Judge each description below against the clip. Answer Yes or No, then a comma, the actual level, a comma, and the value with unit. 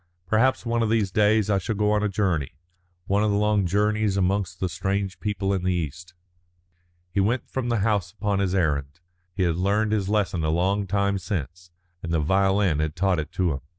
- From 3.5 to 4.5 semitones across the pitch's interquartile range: No, average, 2.8 semitones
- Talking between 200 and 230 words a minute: Yes, fast, 205 wpm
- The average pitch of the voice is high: No, very low, 95 Hz